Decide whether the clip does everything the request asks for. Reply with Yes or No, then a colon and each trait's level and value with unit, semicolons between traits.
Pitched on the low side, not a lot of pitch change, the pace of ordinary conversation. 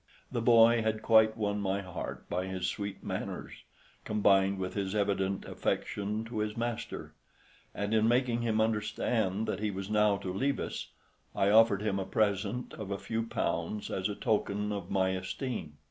Yes: low, 105 Hz; narrow, 2.3 semitones; average, 175 wpm